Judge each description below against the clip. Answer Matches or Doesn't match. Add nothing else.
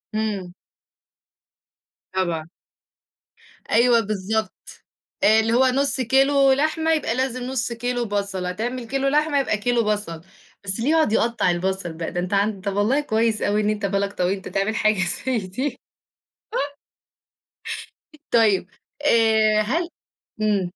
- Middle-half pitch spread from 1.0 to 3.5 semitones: Doesn't match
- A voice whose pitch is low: Doesn't match